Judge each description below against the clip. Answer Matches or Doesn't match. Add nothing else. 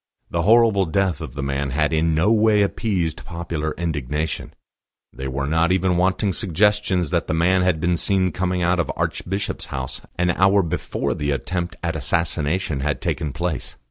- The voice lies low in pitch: Matches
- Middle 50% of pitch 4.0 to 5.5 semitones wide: Doesn't match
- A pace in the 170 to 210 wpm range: Matches